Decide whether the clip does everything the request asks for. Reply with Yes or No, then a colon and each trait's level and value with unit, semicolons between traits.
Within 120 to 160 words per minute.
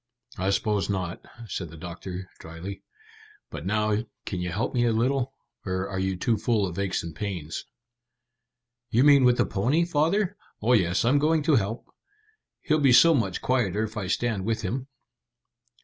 No: average, 175 wpm